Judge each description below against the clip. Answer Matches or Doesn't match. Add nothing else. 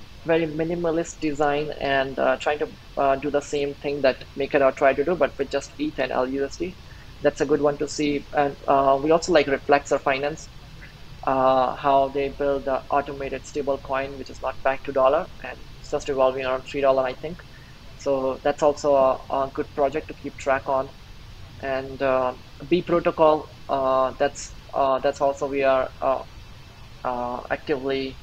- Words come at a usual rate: Matches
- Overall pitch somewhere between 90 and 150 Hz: Matches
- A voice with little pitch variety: Matches